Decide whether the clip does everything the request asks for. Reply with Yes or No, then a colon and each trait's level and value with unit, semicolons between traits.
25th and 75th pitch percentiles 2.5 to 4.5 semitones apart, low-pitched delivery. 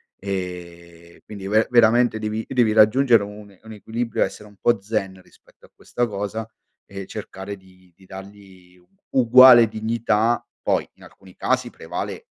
Yes: average, 2.9 semitones; low, 105 Hz